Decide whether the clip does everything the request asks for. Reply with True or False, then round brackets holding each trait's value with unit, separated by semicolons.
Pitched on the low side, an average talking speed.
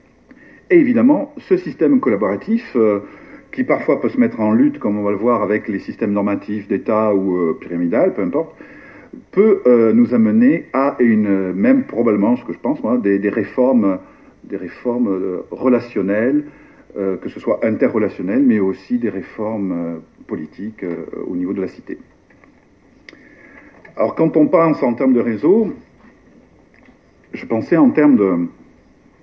True (125 Hz; 160 wpm)